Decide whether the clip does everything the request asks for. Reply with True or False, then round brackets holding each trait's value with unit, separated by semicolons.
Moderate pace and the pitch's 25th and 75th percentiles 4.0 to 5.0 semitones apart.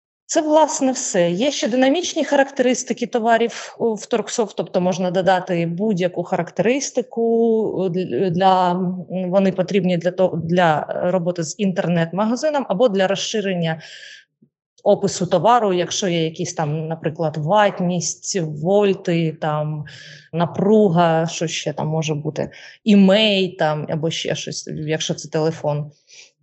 True (115 wpm; 4.5 semitones)